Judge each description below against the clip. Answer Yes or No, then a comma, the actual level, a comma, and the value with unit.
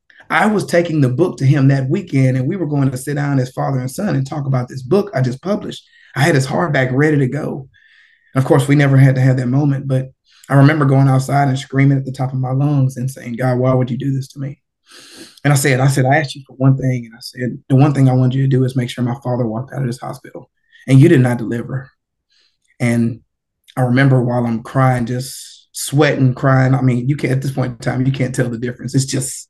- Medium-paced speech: No, fast, 265 wpm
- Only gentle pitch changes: Yes, narrow, 1.7 semitones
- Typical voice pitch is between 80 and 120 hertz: No, low, 130 Hz